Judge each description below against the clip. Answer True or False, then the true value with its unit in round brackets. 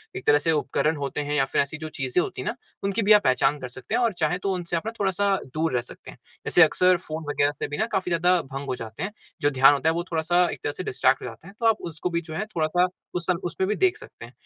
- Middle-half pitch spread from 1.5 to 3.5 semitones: False (4.3 semitones)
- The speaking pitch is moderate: True (160 Hz)